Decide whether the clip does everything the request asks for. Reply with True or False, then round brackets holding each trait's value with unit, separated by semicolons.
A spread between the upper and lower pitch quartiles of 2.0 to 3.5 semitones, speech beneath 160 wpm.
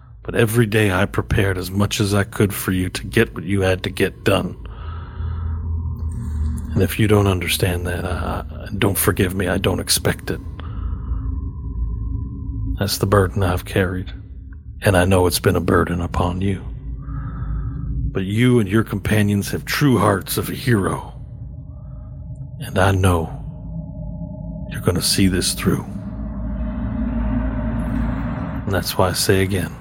True (2.8 semitones; 150 wpm)